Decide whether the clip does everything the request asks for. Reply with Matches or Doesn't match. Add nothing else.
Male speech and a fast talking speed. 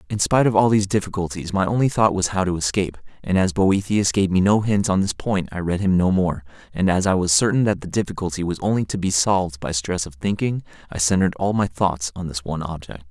Matches